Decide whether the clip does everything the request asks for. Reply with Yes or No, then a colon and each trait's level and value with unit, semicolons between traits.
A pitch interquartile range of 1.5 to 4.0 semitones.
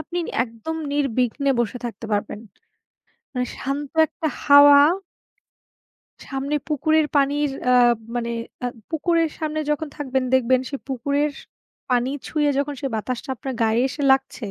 Yes: average, 2.9 semitones